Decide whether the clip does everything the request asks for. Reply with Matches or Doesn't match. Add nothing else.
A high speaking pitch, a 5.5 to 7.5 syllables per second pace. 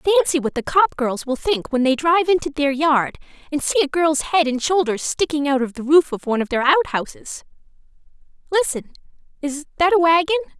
Matches